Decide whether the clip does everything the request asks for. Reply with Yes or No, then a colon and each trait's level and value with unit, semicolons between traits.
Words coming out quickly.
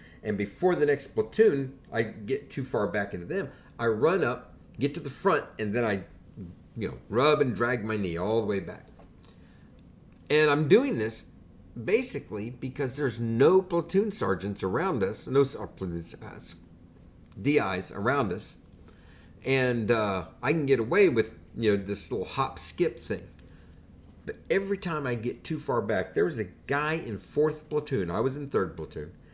No: average, 170 wpm